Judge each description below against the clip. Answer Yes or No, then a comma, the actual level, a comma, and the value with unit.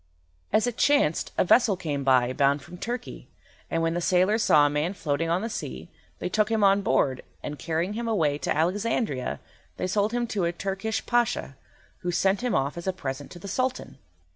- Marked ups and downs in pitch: Yes, wide, 6.5 semitones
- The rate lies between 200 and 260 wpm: Yes, fast, 205 wpm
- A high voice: No, medium, 180 Hz